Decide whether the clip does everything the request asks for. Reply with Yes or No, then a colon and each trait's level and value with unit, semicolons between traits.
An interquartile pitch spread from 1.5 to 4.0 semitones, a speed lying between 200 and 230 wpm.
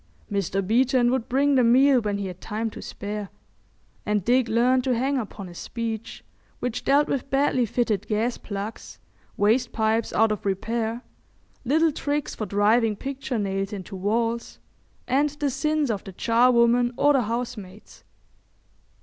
No: average, 3.7 semitones; average, 155 wpm